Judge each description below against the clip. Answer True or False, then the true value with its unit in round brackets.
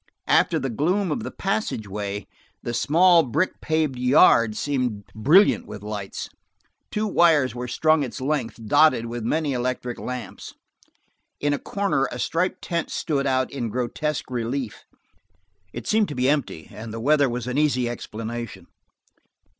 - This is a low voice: True (130 Hz)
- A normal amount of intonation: True (4.6 semitones)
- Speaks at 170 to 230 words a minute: False (150 wpm)